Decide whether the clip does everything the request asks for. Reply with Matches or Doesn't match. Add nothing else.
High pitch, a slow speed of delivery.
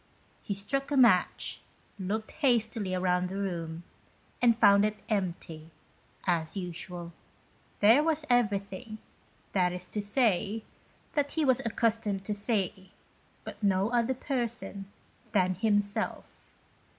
Matches